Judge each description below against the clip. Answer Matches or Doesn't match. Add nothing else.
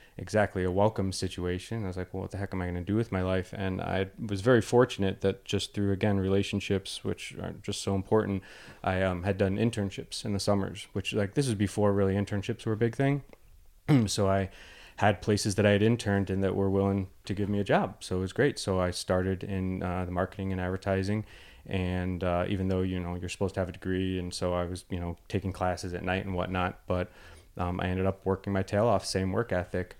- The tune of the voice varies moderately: Doesn't match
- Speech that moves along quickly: Matches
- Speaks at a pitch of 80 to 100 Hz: Matches